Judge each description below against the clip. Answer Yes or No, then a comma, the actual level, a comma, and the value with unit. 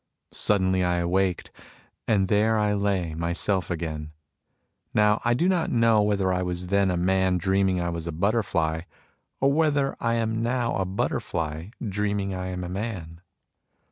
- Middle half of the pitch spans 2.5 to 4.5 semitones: Yes, average, 3.4 semitones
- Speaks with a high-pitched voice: No, very low, 95 Hz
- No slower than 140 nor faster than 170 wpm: Yes, average, 160 wpm